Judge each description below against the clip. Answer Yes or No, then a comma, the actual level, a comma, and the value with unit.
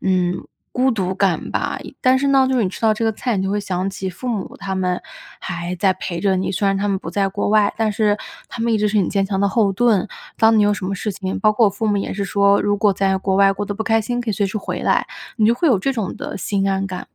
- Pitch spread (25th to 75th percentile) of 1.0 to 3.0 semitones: Yes, narrow, 2.4 semitones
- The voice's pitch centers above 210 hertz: No, high, 200 Hz